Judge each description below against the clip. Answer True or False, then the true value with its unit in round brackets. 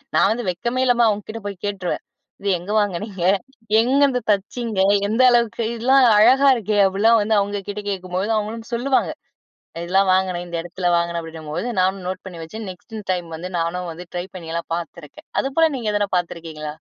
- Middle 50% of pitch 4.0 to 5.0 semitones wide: True (4.3 semitones)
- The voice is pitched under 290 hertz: True (200 Hz)